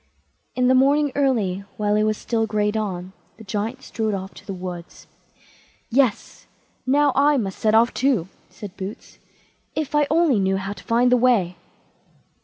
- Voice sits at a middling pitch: No, high, 220 Hz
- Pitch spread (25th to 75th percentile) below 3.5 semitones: No, average, 4.9 semitones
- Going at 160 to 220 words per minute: Yes, average, 170 wpm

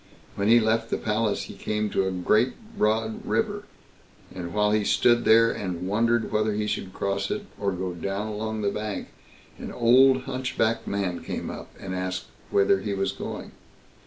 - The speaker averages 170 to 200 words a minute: Yes, average, 180 wpm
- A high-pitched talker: No, low, 105 Hz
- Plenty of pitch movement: No, average, 2.7 semitones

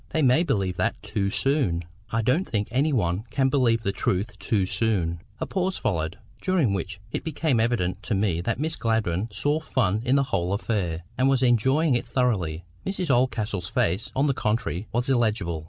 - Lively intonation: Yes, wide, 5.7 semitones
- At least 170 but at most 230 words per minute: Yes, average, 190 wpm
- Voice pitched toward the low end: Yes, low, 115 Hz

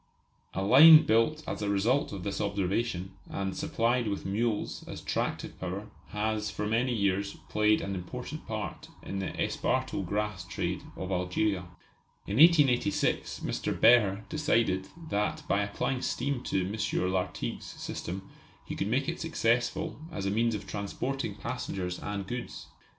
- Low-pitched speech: Yes, low, 105 Hz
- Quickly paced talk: No, average, 150 wpm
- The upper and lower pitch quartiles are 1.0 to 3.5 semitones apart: No, average, 4.0 semitones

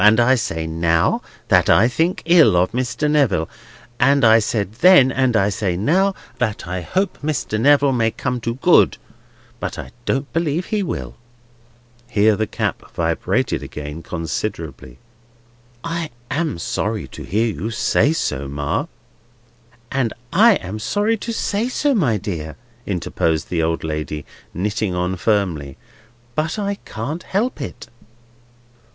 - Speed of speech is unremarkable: Yes, average, 145 wpm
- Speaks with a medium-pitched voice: No, low, 115 Hz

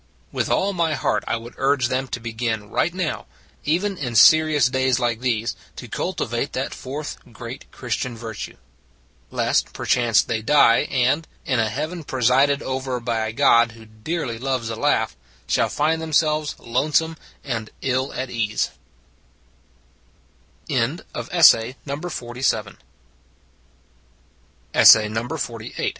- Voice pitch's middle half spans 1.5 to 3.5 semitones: No, average, 4.3 semitones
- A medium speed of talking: No, slow, 120 wpm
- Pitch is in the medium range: No, low, 130 Hz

